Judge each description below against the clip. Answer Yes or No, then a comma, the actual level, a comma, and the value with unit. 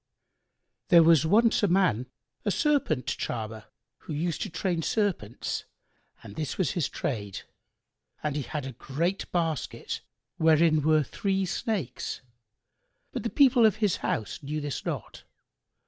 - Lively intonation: Yes, wide, 6.0 semitones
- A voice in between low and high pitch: Yes, medium, 160 Hz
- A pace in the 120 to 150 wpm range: Yes, average, 140 wpm